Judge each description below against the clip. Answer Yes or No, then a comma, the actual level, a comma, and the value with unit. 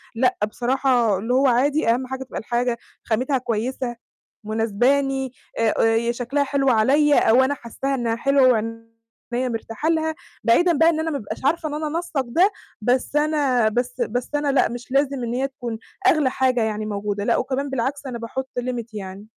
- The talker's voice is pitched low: No, very high, 255 Hz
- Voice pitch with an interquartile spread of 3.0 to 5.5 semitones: Yes, average, 3.3 semitones